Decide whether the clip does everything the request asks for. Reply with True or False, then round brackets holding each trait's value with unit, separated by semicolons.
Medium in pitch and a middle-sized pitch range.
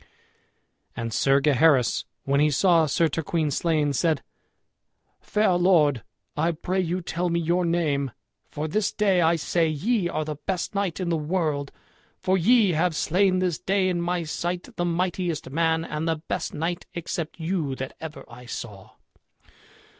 True (165 Hz; 3.0 semitones)